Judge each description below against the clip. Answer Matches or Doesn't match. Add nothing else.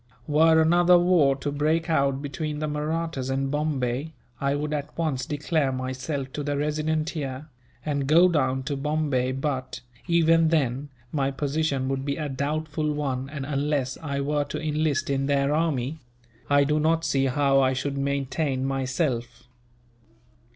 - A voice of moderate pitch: Matches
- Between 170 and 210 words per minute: Doesn't match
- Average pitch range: Doesn't match